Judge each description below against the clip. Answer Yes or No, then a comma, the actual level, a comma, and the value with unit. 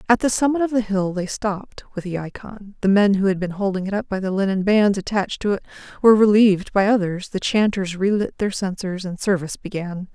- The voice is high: Yes, high, 200 Hz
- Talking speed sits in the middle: No, fast, 225 wpm